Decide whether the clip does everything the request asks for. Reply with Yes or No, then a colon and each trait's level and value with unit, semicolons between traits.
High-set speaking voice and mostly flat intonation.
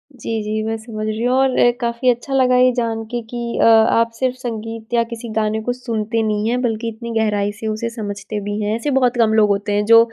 Yes: high, 225 Hz; narrow, 1.9 semitones